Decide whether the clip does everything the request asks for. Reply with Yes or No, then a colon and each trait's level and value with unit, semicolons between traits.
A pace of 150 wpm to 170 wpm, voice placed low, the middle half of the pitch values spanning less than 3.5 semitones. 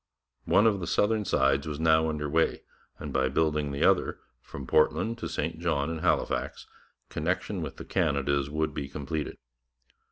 Yes: average, 165 wpm; very low, 75 Hz; narrow, 2.6 semitones